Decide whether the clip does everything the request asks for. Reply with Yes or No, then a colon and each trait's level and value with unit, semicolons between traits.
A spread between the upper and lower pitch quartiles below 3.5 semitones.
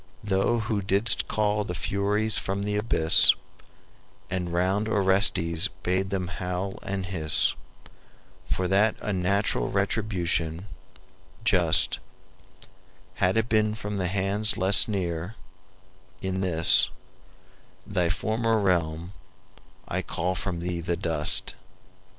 Yes: average, 2.7 semitones